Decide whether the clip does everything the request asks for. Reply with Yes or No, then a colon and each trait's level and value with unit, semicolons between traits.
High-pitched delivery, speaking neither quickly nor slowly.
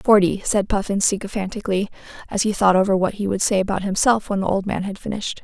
No: high, 200 Hz; fast, 220 wpm